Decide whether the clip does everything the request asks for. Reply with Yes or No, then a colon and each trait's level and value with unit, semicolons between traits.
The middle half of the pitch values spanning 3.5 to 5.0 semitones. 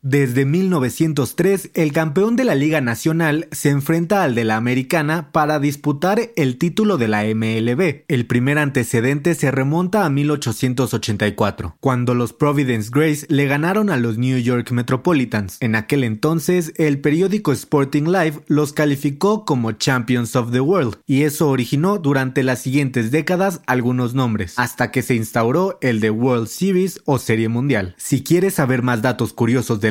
Yes: average, 4.6 semitones